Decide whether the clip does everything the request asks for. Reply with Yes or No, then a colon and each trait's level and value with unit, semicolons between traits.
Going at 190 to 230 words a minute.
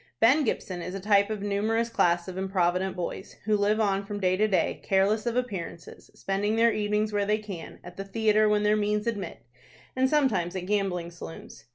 Yes: fast, 205 wpm